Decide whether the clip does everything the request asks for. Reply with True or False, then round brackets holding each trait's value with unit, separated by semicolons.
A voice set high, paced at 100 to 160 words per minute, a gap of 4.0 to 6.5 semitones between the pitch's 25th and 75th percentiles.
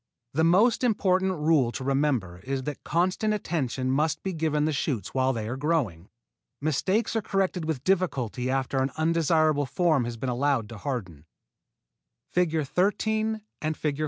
False (150 Hz; 150 wpm; 5.4 semitones)